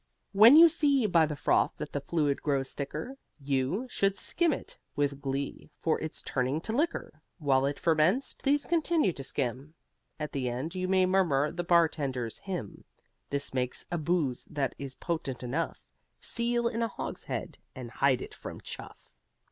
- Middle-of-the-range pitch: Yes, medium, 155 Hz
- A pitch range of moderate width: No, wide, 6.3 semitones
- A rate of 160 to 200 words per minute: Yes, average, 170 wpm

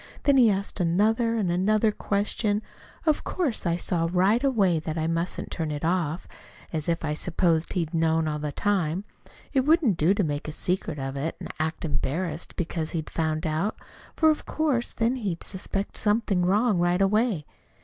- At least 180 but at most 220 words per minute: Yes, average, 190 wpm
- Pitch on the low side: No, medium, 180 Hz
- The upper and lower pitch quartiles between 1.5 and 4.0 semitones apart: No, average, 4.8 semitones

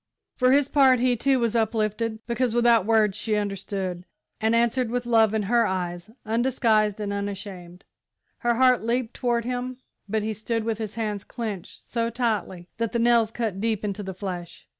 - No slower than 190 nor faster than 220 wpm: No, average, 180 wpm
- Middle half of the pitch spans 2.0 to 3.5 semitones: Yes, average, 2.8 semitones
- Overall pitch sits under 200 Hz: No, high, 225 Hz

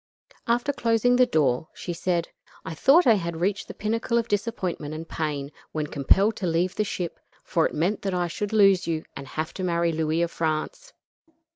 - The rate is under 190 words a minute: No, average, 195 wpm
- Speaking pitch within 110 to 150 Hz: No, medium, 175 Hz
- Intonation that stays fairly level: No, average, 5.2 semitones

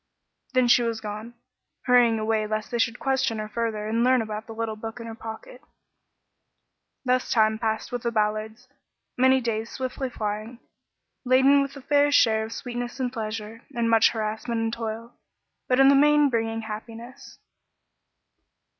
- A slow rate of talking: No, average, 170 wpm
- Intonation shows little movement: Yes, narrow, 2.3 semitones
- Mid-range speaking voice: No, high, 230 Hz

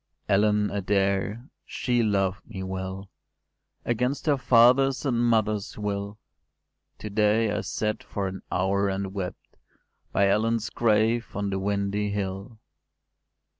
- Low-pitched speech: Yes, low, 105 Hz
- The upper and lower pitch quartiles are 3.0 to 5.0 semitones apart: No, narrow, 2.6 semitones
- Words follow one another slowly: Yes, slow, 125 wpm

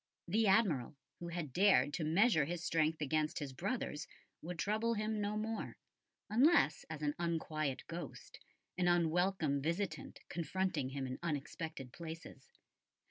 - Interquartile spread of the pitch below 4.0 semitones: No, average, 4.6 semitones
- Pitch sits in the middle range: Yes, medium, 165 Hz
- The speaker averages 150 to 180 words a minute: No, slow, 135 wpm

